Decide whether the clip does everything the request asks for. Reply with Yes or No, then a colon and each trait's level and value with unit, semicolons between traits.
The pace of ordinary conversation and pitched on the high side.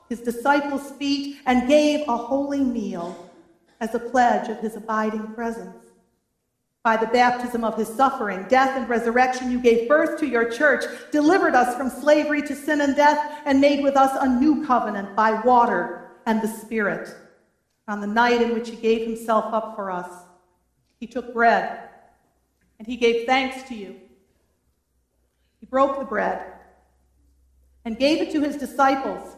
Yes: average, 165 wpm; high, 235 Hz